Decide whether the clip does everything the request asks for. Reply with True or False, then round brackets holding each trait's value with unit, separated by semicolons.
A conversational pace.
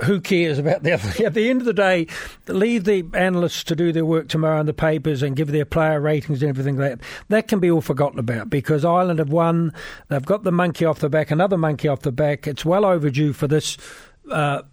False (240 wpm)